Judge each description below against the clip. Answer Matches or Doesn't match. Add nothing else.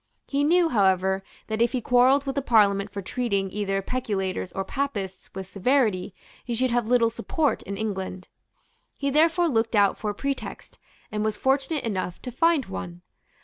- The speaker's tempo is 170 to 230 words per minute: Matches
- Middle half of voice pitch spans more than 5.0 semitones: Matches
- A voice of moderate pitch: Doesn't match